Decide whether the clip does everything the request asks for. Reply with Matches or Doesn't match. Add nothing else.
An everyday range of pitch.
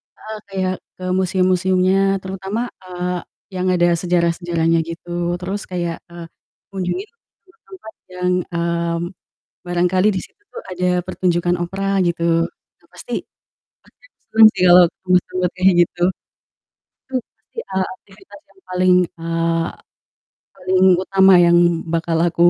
Doesn't match